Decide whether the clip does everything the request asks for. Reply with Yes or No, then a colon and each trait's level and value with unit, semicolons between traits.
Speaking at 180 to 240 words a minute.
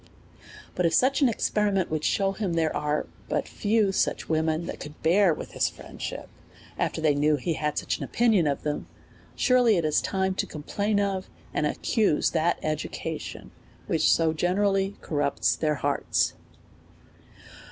No: average, 170 wpm